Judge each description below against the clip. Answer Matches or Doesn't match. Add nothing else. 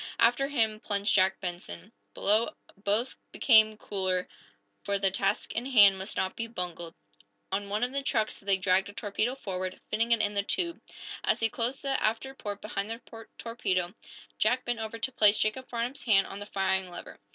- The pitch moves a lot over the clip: Doesn't match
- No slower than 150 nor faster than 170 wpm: Doesn't match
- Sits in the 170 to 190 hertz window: Doesn't match